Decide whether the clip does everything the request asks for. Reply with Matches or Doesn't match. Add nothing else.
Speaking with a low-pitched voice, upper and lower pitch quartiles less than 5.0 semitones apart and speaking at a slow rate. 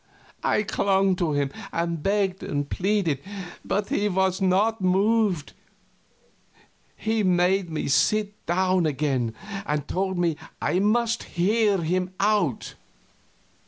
Doesn't match